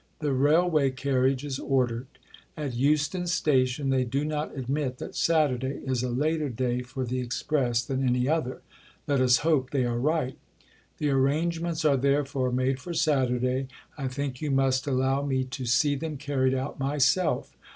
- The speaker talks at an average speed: Yes, average, 165 wpm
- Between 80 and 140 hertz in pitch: Yes, low, 135 Hz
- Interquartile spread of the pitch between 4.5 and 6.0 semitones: No, narrow, 2.6 semitones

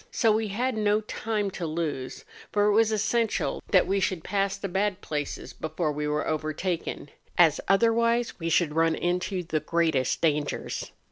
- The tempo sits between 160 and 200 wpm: Yes, average, 165 wpm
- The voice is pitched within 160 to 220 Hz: Yes, medium, 185 Hz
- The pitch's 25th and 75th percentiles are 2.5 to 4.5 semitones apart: No, average, 4.9 semitones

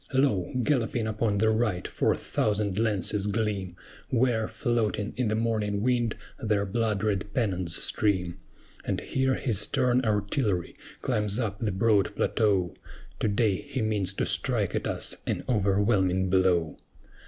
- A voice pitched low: Yes, low, 105 Hz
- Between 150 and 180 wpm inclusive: No, average, 140 wpm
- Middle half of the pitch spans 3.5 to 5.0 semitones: No, average, 2.8 semitones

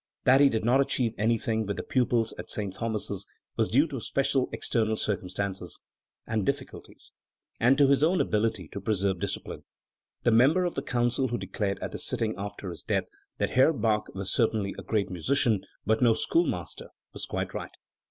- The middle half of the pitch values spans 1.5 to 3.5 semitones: No, average, 4.2 semitones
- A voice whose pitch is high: No, low, 110 Hz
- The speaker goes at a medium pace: Yes, average, 180 wpm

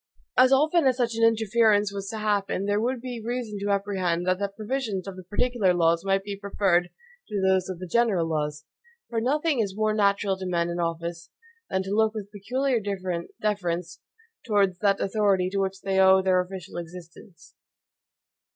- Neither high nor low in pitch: No, high, 200 Hz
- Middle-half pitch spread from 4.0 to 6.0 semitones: No, average, 3.2 semitones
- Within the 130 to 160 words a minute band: No, average, 180 wpm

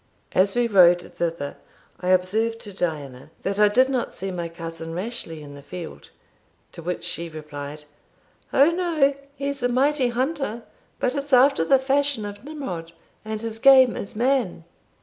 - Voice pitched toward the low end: No, high, 210 Hz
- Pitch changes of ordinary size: No, wide, 7.7 semitones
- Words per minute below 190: Yes, average, 165 wpm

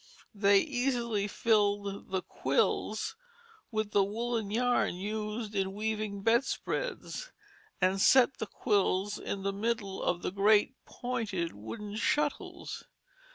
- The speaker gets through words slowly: Yes, slow, 115 wpm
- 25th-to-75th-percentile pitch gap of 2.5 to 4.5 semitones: Yes, average, 2.8 semitones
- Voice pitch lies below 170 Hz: No, high, 210 Hz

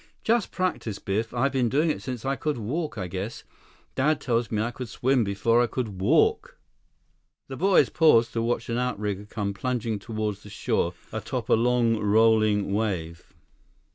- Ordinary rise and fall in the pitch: Yes, average, 3.7 semitones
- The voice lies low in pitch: Yes, low, 115 Hz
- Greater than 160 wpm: Yes, average, 170 wpm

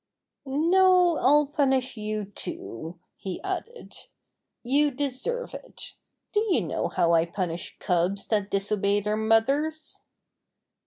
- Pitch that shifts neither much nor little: No, wide, 7.1 semitones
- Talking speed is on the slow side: Yes, slow, 115 wpm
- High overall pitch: Yes, very high, 250 Hz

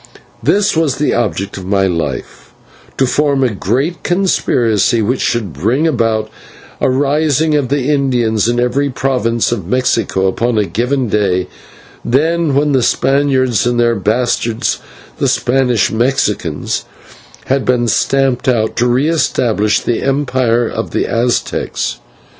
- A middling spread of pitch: Yes, average, 3.9 semitones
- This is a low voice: Yes, low, 120 Hz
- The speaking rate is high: No, average, 140 wpm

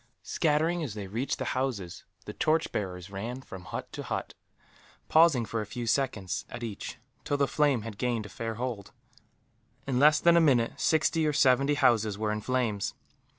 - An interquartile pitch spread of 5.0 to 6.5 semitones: Yes, average, 5.3 semitones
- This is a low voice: Yes, low, 125 Hz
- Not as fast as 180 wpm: No, average, 185 wpm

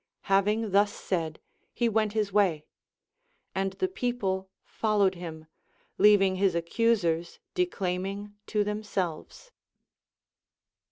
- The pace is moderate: No, slow, 105 wpm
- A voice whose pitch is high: Yes, high, 200 Hz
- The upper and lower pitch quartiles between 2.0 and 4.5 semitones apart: Yes, narrow, 2.6 semitones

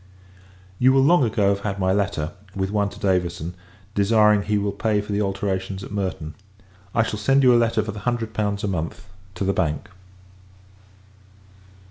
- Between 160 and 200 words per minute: Yes, average, 180 wpm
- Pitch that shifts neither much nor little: No, narrow, 2.2 semitones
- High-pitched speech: No, low, 100 Hz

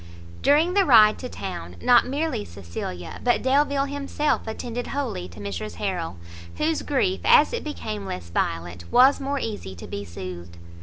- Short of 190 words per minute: Yes, average, 160 wpm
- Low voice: No, high, 220 Hz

